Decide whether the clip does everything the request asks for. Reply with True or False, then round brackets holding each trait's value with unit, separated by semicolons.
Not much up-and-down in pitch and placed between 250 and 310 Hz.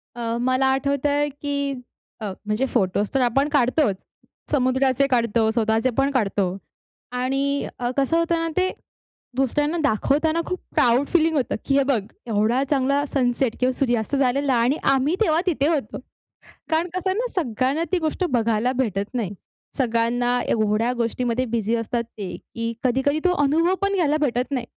False (3.6 semitones; 260 Hz)